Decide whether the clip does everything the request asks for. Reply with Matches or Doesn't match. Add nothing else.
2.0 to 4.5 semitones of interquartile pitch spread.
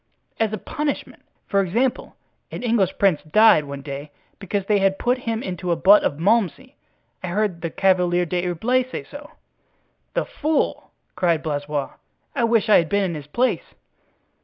Doesn't match